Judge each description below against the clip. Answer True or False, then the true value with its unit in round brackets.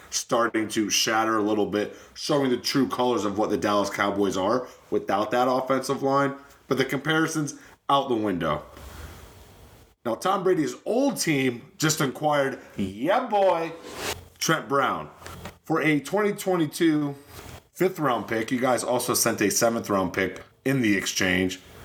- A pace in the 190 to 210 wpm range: False (150 wpm)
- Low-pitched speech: True (125 Hz)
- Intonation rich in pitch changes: True (6.0 semitones)